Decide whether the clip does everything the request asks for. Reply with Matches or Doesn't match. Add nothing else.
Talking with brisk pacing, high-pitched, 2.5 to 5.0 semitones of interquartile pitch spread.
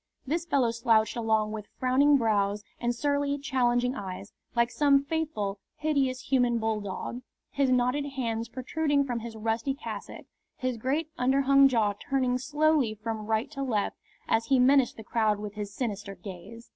Doesn't match